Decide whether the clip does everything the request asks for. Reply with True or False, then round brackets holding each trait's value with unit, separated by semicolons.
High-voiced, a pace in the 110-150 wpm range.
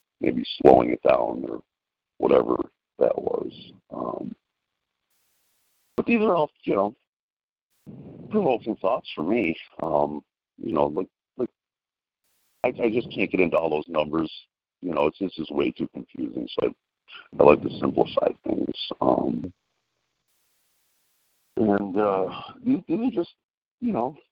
False (170 Hz; 140 wpm)